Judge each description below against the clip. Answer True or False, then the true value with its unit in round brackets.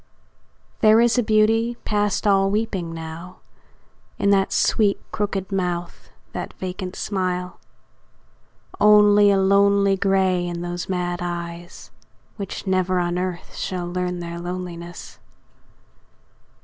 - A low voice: False (185 Hz)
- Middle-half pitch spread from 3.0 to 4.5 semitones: False (2.4 semitones)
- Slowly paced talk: True (115 wpm)